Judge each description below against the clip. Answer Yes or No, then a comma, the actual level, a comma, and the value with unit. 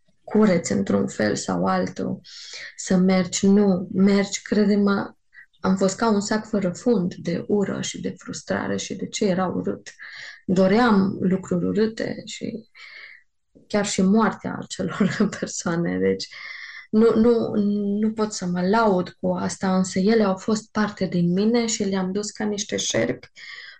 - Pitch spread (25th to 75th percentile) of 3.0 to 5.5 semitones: No, narrow, 2.6 semitones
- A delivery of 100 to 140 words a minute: No, average, 150 wpm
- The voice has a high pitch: Yes, high, 200 Hz